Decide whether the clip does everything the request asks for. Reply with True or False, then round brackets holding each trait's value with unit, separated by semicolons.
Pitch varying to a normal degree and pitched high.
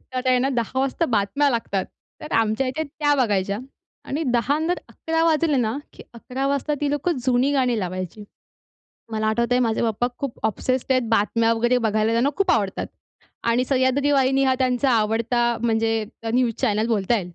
True (3.5 semitones; 245 Hz)